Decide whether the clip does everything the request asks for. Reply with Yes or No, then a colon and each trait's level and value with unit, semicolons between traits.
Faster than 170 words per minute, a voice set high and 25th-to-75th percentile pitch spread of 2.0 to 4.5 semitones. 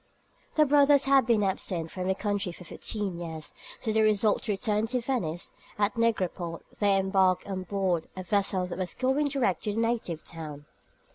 Yes: average, 190 wpm; high, 200 Hz; average, 3.9 semitones